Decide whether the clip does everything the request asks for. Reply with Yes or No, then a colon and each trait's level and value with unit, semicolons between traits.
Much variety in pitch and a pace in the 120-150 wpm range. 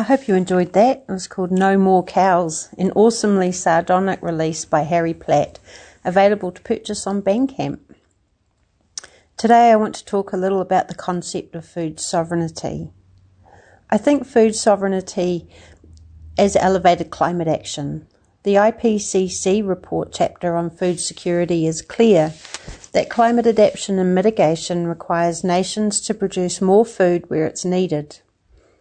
No: average, 3.2 semitones; average, 140 wpm